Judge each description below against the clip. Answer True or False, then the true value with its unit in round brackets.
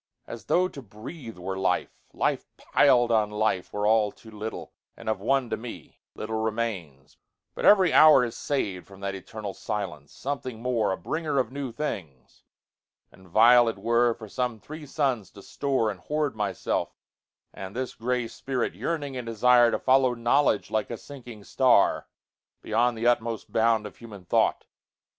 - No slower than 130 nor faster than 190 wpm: True (150 wpm)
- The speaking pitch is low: True (115 Hz)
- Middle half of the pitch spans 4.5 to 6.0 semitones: False (3.6 semitones)